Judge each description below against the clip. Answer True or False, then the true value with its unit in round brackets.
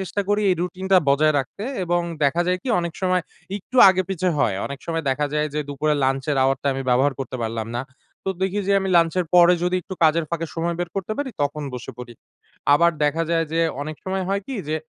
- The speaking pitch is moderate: True (165 Hz)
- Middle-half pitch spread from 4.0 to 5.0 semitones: True (4.3 semitones)